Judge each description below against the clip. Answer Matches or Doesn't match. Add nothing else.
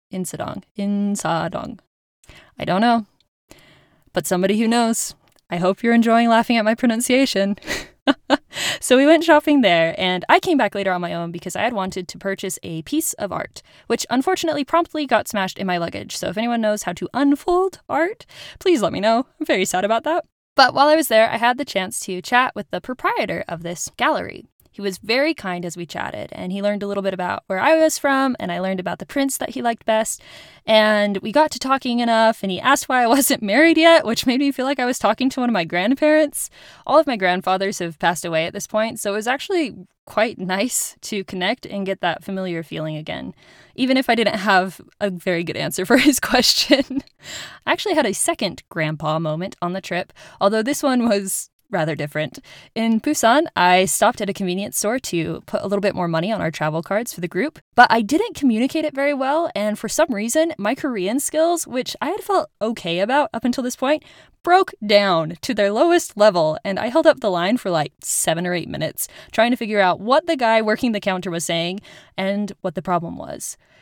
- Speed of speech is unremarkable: Doesn't match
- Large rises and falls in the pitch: Matches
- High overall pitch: Matches